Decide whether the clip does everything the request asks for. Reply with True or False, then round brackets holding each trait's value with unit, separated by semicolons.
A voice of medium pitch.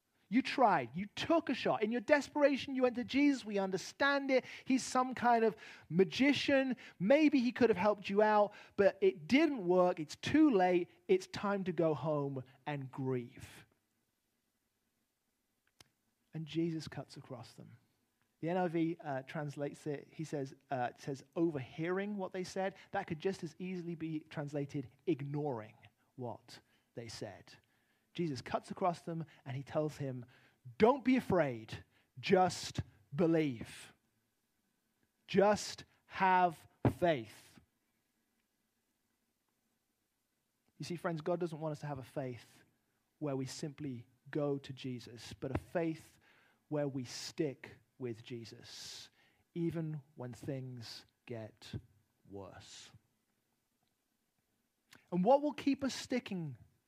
True (155 Hz)